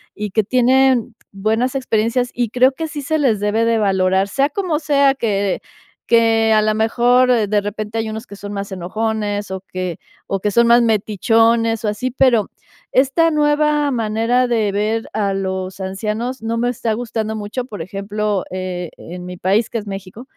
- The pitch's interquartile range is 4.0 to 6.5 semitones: No, average, 3.3 semitones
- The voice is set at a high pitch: Yes, high, 220 Hz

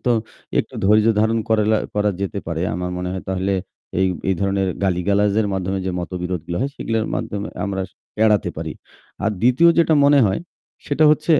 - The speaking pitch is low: Yes, low, 100 Hz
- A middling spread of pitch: Yes, average, 3.0 semitones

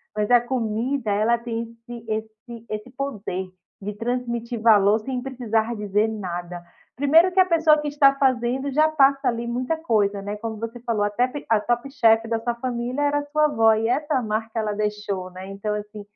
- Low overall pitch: No, high, 230 Hz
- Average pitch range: Yes, average, 3.5 semitones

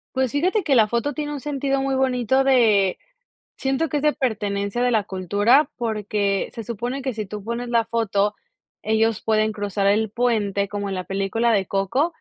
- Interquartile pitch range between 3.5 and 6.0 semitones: Yes, average, 4.5 semitones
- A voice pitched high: Yes, high, 225 Hz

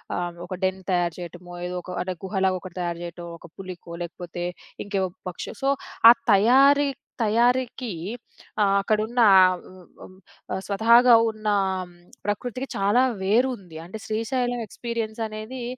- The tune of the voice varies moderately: Yes, average, 4.7 semitones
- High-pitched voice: Yes, high, 205 Hz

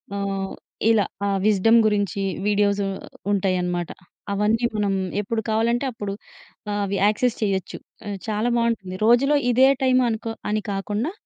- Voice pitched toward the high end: Yes, high, 210 Hz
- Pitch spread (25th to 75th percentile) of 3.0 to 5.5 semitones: No, narrow, 2.5 semitones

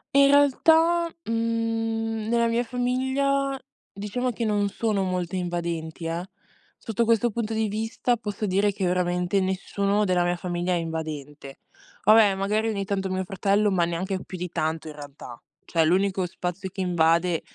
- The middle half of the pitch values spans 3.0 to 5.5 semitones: Yes, average, 4.2 semitones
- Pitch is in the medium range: No, high, 195 Hz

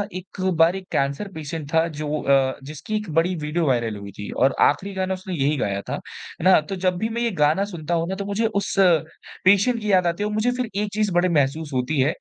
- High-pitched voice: No, medium, 170 Hz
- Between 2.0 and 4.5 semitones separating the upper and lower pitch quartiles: No, average, 5.1 semitones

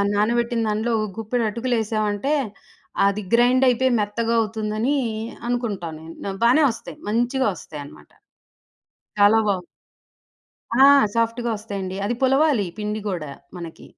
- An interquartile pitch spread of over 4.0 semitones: No, average, 2.8 semitones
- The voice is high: Yes, high, 220 Hz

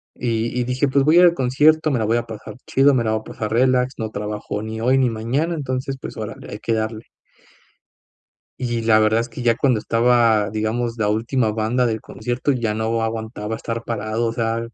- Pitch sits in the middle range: No, low, 115 Hz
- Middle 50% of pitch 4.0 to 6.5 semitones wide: No, narrow, 2.5 semitones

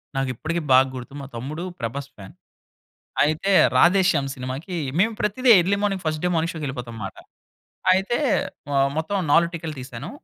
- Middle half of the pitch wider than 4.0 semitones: Yes, average, 5.3 semitones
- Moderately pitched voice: Yes, medium, 155 Hz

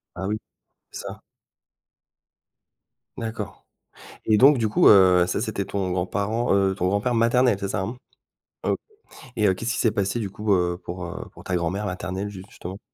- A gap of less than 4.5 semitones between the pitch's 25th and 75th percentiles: Yes, average, 2.9 semitones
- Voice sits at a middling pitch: No, low, 100 Hz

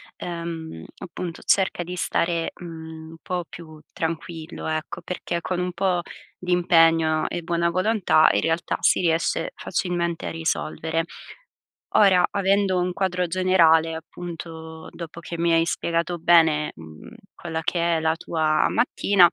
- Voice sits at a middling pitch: Yes, medium, 170 Hz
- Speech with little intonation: Yes, narrow, 1.7 semitones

